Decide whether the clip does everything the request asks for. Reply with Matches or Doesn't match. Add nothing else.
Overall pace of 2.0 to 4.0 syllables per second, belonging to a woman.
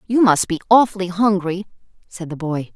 Doesn't match